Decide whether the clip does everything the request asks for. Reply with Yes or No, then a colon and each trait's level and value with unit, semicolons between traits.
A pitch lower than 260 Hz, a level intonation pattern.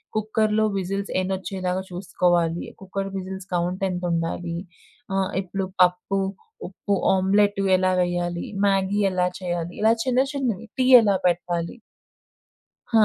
Yes: high, 190 Hz; narrow, 2.0 semitones